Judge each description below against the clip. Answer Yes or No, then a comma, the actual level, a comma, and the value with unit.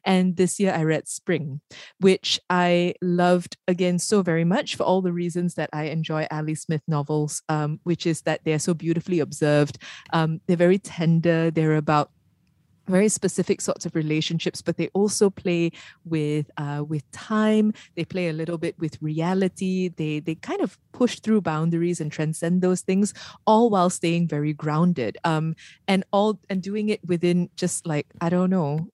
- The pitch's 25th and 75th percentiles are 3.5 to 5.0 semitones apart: No, average, 2.9 semitones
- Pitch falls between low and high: Yes, medium, 170 Hz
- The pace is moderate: Yes, average, 175 wpm